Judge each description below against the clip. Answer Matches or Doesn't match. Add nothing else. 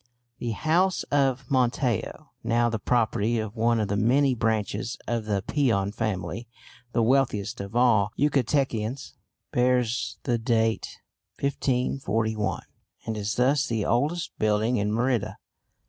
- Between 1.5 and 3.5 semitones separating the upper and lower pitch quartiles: Matches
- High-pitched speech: Doesn't match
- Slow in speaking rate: Matches